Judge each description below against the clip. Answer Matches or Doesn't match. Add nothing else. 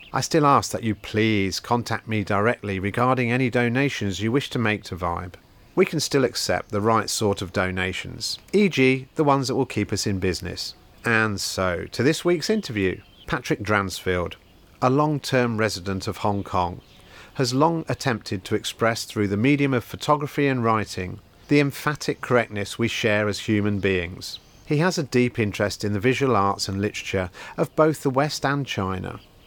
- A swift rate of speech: Doesn't match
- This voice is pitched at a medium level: Doesn't match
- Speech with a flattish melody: Doesn't match